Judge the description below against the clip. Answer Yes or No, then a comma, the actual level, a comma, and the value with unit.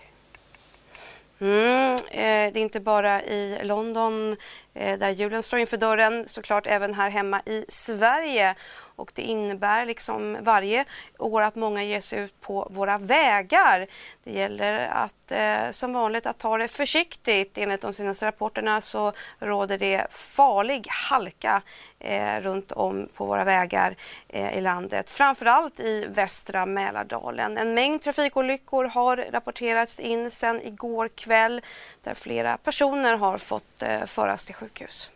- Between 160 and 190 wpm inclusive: No, average, 145 wpm